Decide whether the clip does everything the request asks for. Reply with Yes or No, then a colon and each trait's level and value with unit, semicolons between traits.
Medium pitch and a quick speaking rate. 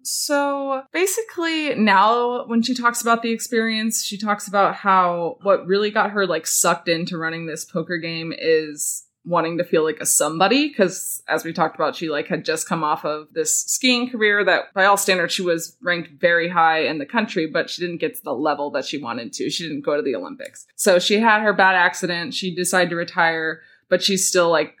Yes: medium, 180 Hz; fast, 215 wpm